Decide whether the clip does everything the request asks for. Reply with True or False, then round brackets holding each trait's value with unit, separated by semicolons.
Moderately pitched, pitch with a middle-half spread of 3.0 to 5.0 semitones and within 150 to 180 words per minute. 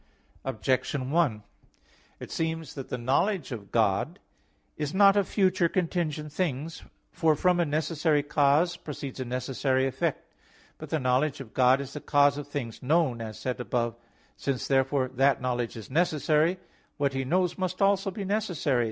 True (145 Hz; 4.5 semitones; 170 wpm)